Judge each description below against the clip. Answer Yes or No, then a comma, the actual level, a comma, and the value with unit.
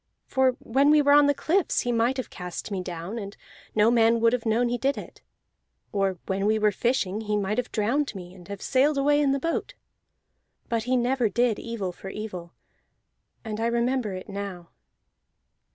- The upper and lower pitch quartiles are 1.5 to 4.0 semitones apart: No, average, 4.5 semitones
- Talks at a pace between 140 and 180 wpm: No, average, 195 wpm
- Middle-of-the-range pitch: No, high, 230 Hz